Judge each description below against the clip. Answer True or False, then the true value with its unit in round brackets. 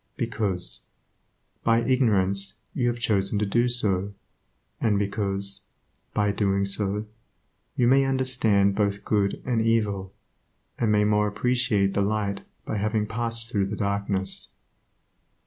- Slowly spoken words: True (130 wpm)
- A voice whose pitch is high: False (105 Hz)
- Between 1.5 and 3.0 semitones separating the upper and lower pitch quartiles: True (2.6 semitones)